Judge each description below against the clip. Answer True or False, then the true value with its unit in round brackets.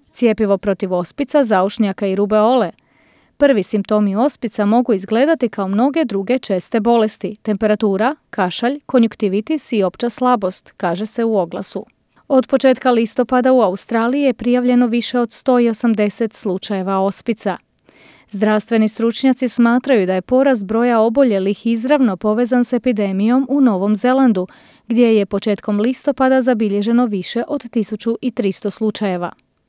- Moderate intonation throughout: True (3.5 semitones)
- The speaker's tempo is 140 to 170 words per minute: False (125 wpm)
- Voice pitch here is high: True (230 Hz)